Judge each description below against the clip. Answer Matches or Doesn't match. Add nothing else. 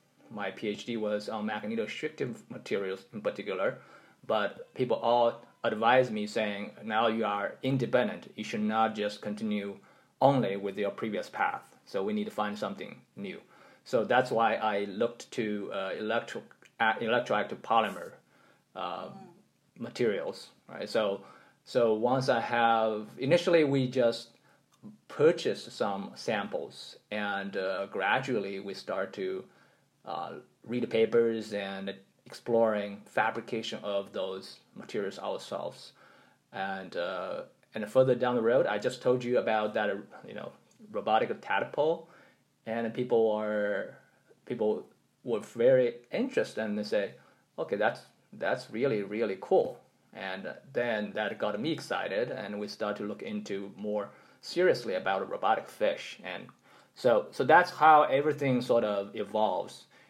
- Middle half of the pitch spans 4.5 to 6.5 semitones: Doesn't match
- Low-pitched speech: Matches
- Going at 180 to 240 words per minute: Doesn't match